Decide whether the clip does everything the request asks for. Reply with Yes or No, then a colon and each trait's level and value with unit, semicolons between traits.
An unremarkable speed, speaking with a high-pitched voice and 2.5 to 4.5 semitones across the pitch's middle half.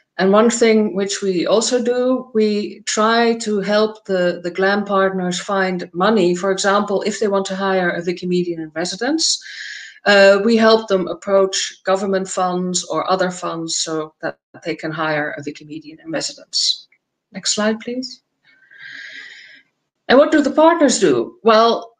No: fast, 155 wpm; high, 195 Hz; average, 3.6 semitones